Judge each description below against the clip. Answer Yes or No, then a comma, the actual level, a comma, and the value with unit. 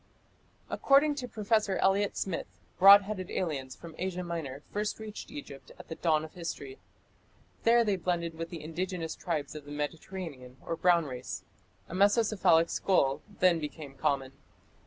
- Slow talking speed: No, average, 155 wpm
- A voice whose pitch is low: No, medium, 170 Hz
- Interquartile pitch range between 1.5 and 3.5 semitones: No, average, 4.5 semitones